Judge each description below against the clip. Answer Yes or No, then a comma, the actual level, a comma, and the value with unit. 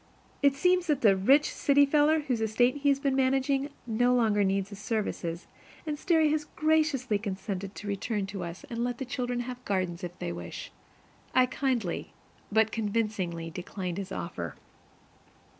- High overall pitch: Yes, high, 230 Hz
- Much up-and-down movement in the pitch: Yes, wide, 5.9 semitones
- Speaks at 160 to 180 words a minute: Yes, average, 165 wpm